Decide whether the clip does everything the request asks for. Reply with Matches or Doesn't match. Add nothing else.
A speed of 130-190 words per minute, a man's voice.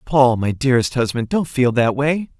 Doesn't match